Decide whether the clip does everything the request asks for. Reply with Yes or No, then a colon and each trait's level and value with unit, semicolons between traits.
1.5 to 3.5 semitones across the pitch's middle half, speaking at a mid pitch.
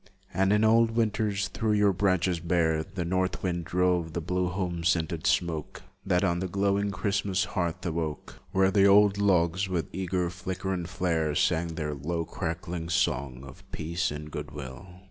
No: average, 2.7 semitones; very low, 90 Hz